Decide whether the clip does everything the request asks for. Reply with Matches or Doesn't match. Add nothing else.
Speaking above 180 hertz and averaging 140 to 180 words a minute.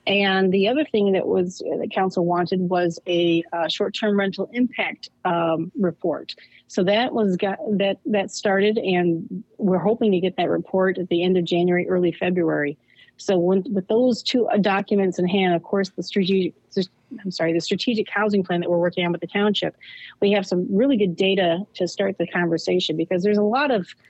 Doesn't match